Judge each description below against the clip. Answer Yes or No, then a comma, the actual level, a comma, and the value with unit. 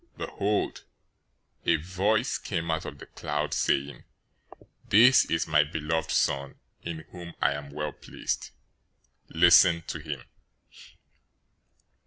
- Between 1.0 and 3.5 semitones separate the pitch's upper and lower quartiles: Yes, average, 2.8 semitones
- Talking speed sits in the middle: No, slow, 115 wpm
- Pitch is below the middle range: Yes, very low, 80 Hz